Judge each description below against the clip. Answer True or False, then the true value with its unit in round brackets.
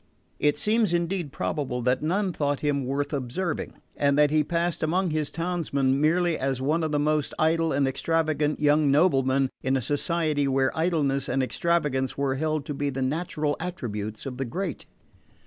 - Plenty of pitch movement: False (3.4 semitones)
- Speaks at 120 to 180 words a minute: True (175 wpm)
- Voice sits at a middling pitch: True (150 Hz)